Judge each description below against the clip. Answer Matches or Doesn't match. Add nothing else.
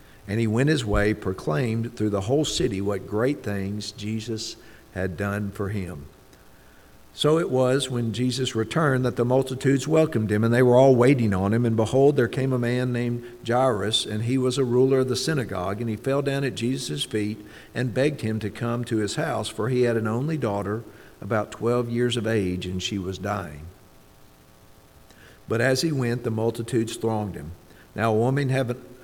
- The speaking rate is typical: Matches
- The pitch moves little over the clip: Doesn't match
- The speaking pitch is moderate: Doesn't match